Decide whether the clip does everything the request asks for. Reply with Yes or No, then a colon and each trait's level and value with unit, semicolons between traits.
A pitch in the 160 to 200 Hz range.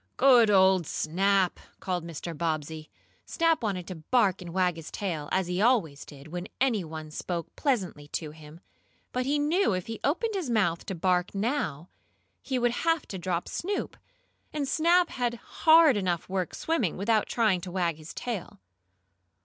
Yes: high, 190 Hz